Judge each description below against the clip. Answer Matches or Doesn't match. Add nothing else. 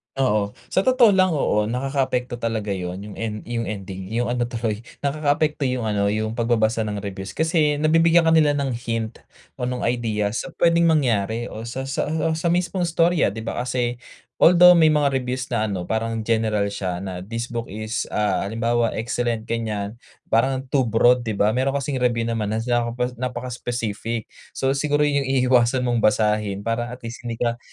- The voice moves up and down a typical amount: Matches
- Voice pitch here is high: Doesn't match